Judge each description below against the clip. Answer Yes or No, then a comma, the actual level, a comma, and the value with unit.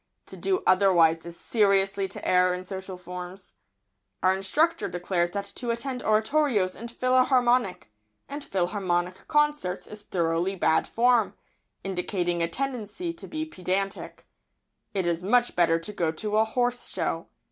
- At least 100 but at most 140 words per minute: Yes, slow, 135 wpm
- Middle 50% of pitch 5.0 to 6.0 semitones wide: Yes, average, 5.3 semitones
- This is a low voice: No, high, 195 Hz